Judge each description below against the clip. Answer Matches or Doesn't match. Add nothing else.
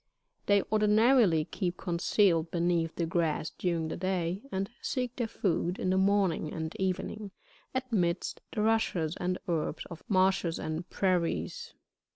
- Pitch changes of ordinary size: Matches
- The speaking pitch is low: Doesn't match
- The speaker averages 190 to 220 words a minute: Doesn't match